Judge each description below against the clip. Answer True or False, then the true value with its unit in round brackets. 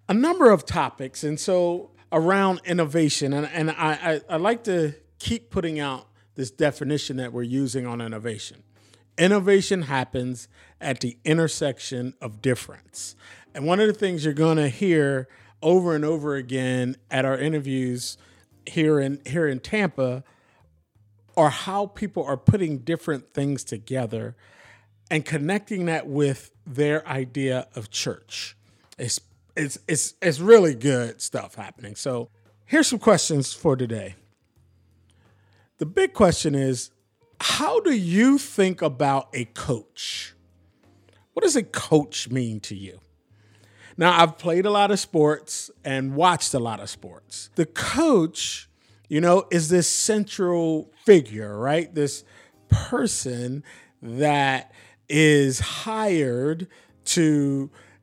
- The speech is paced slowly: True (130 wpm)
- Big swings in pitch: True (6.3 semitones)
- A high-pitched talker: False (140 Hz)